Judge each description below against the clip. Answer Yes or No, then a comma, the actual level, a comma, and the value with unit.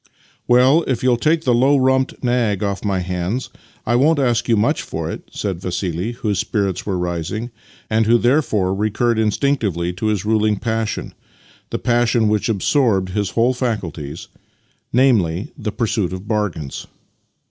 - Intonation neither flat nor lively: Yes, average, 4.1 semitones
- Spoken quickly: No, average, 165 wpm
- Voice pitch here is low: Yes, low, 110 Hz